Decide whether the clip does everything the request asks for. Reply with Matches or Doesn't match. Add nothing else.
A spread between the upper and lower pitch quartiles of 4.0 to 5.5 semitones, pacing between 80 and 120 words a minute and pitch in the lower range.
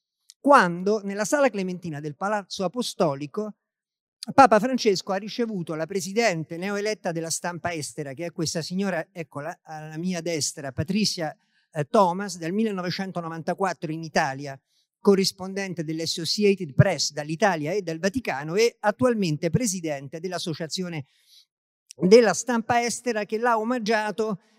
Doesn't match